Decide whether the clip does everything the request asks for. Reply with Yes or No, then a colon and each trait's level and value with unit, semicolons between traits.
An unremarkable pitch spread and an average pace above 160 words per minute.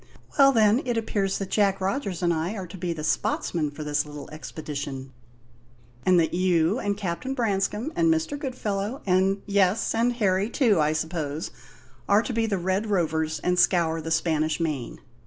Yes: average, 5.0 semitones; average, 175 wpm